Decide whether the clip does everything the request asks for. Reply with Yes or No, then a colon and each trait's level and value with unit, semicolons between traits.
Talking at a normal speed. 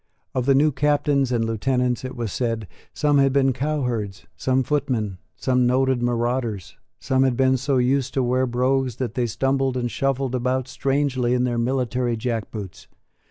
Yes: average, 175 wpm